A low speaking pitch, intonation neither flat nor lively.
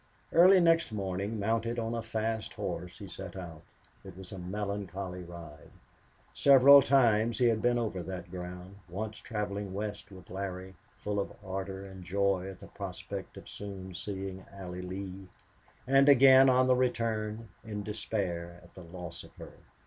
Yes: low, 100 Hz; average, 3.5 semitones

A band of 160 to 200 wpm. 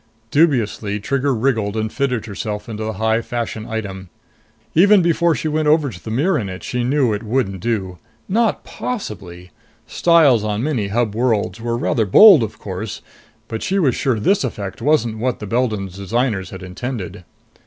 Yes: average, 175 wpm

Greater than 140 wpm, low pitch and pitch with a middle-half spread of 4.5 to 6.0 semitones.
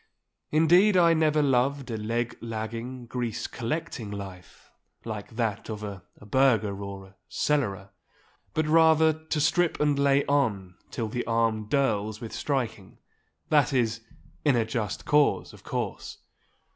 No: slow, 135 wpm; low, 120 Hz; average, 5.3 semitones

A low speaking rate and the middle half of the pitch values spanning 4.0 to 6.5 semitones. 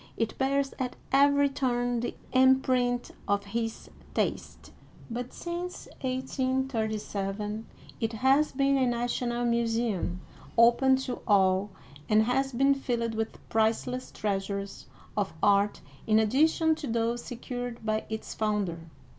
No: slow, 120 wpm; average, 3.4 semitones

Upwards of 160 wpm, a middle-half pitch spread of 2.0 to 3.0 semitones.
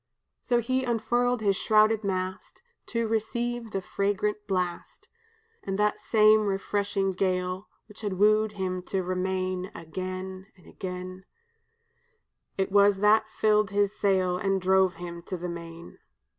No: slow, 135 wpm; narrow, 2.4 semitones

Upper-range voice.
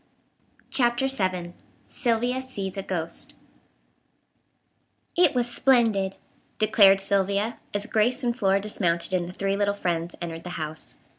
Yes: high, 200 Hz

